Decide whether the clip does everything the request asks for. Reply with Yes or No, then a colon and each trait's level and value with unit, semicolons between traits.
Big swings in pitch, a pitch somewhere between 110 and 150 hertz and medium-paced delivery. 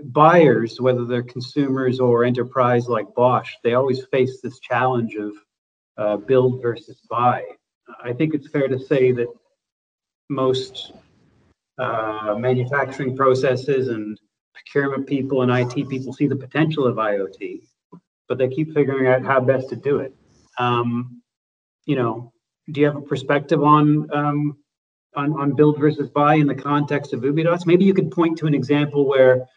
No: average, 2.9 semitones; low, 130 Hz; average, 160 wpm